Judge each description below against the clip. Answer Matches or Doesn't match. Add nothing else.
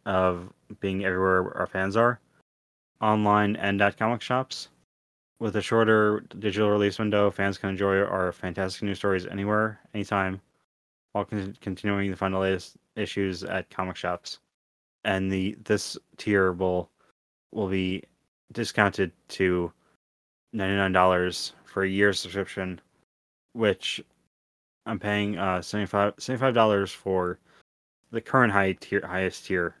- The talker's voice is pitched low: Matches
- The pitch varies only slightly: Matches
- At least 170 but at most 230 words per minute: Doesn't match